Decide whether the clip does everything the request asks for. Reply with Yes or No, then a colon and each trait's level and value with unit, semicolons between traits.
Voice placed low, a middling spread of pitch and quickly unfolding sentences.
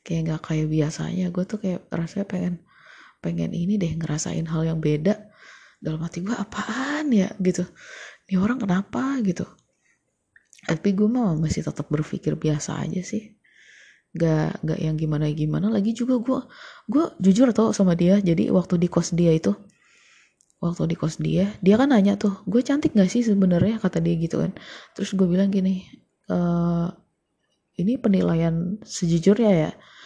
No: medium, 185 Hz; average, 4.1 semitones; fast, 160 wpm